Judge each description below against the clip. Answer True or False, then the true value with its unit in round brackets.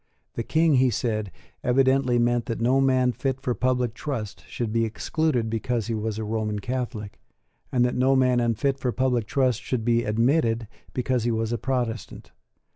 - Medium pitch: False (120 Hz)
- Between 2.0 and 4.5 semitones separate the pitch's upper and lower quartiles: True (2.4 semitones)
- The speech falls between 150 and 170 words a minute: False (180 wpm)